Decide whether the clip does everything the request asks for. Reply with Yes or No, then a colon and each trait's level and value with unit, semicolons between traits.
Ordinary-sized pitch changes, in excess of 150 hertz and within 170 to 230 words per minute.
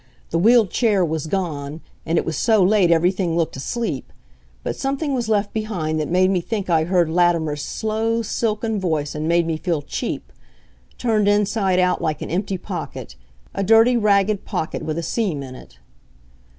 Yes: average, 5.0 semitones; medium, 185 Hz; average, 175 wpm